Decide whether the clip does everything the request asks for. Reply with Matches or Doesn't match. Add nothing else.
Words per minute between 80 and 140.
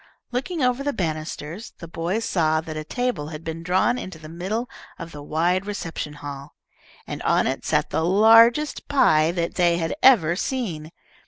Doesn't match